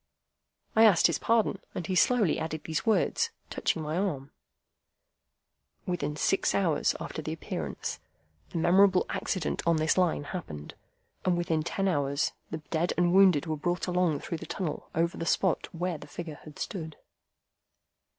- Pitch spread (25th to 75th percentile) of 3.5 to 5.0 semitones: No, average, 3.0 semitones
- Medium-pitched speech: Yes, medium, 170 Hz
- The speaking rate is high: No, average, 160 wpm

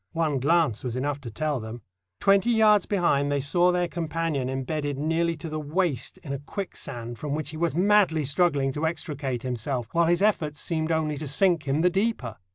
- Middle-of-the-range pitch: Yes, medium, 155 Hz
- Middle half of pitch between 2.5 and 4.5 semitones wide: Yes, average, 3.8 semitones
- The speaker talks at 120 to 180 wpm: No, average, 195 wpm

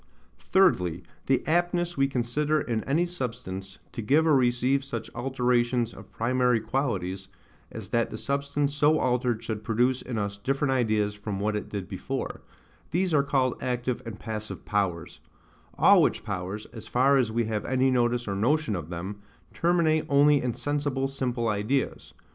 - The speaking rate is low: No, average, 165 wpm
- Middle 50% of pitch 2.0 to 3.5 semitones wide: No, average, 4.5 semitones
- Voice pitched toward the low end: Yes, low, 125 Hz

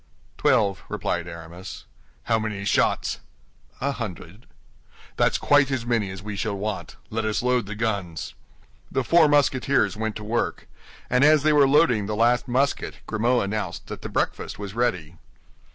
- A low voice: Yes, low, 110 Hz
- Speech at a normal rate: Yes, average, 160 wpm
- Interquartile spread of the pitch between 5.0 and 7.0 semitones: No, average, 4.1 semitones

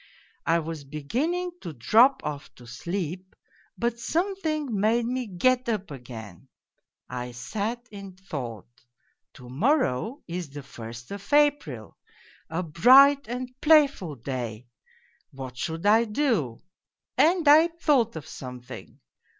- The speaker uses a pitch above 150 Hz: Yes, high, 190 Hz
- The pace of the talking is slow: Yes, slow, 125 wpm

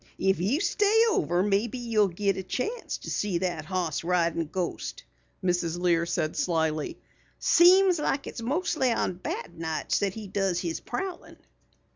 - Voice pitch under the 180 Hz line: No, high, 190 Hz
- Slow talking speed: No, average, 155 wpm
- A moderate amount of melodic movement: No, wide, 7.1 semitones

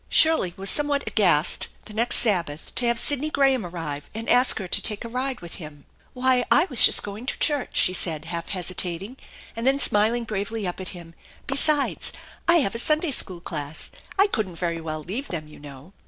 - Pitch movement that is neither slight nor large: No, wide, 7.1 semitones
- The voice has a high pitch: Yes, high, 205 Hz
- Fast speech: Yes, fast, 210 wpm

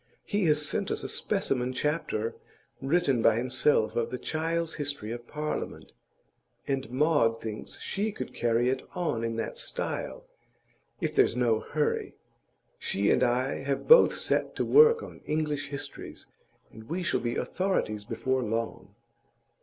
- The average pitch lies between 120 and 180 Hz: Yes, low, 135 Hz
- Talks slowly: No, average, 150 wpm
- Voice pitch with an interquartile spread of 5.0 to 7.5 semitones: Yes, average, 5.3 semitones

